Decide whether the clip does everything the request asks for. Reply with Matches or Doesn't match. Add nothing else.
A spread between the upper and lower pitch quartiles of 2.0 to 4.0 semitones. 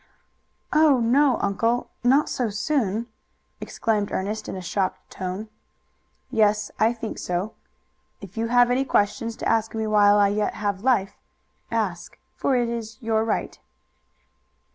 Matches